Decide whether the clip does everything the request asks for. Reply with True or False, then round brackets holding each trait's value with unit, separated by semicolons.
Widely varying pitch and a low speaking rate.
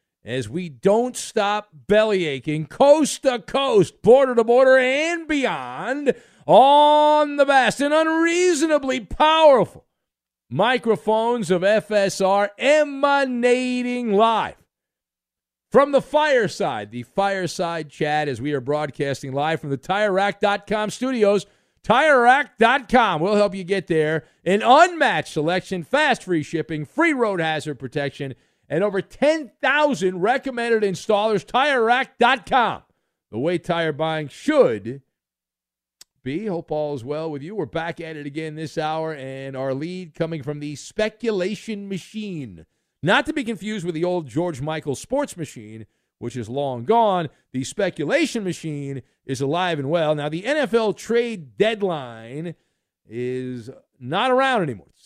True (8.3 semitones; 130 wpm)